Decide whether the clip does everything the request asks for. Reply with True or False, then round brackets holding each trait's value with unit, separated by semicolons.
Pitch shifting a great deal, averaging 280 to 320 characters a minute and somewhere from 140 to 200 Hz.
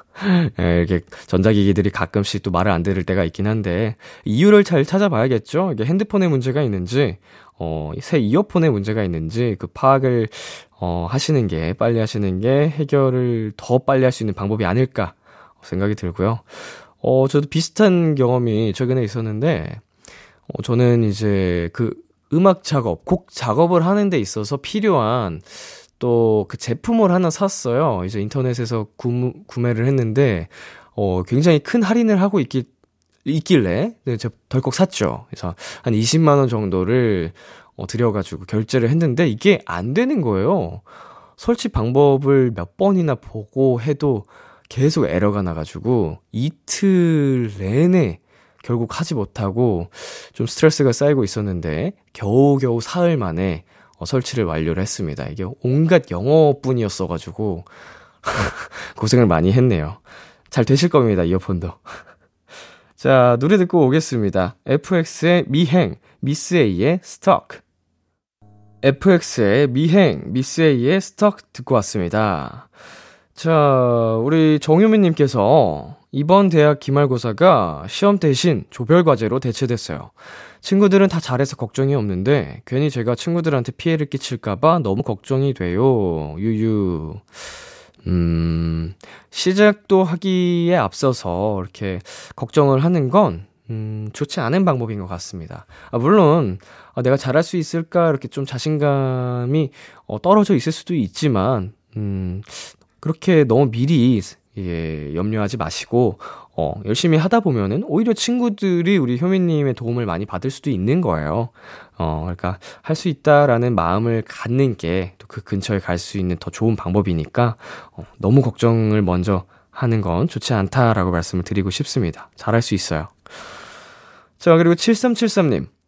False (7.4 semitones; 285 characters per minute; 125 Hz)